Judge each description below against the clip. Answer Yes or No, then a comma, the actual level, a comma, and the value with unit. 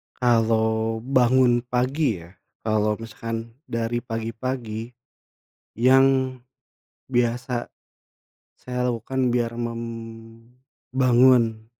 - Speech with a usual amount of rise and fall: No, narrow, 1.9 semitones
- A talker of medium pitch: No, low, 120 Hz